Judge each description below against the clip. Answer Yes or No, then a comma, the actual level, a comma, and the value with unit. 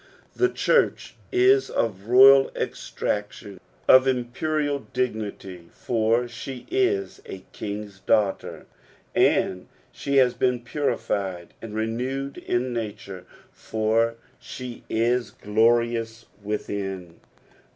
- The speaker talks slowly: Yes, slow, 100 wpm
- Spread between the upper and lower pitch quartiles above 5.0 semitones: No, average, 3.9 semitones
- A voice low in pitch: Yes, low, 115 Hz